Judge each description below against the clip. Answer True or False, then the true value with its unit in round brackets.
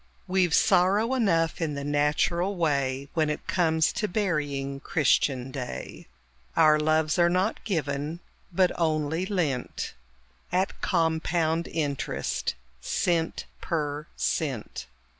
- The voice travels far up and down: False (3.3 semitones)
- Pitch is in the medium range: True (160 Hz)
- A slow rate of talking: True (115 wpm)